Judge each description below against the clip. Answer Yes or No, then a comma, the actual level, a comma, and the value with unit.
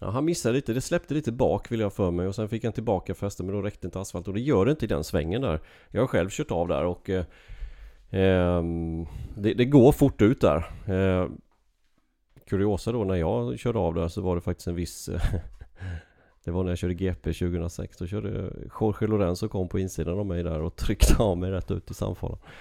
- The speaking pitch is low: Yes, very low, 95 Hz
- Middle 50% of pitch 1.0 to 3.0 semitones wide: No, average, 3.4 semitones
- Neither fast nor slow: No, fast, 235 wpm